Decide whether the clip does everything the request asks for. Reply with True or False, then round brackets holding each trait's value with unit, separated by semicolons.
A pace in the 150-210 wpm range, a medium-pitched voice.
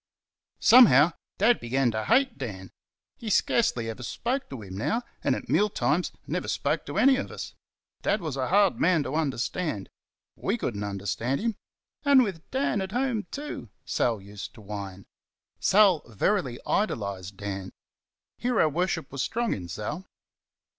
True (160 wpm; 150 Hz)